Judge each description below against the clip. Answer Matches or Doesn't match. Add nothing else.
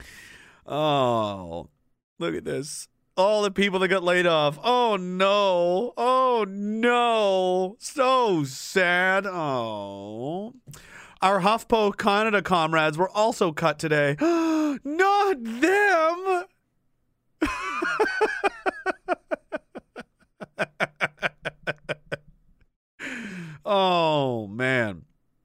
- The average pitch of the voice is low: Doesn't match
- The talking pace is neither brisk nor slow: Doesn't match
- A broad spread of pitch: Matches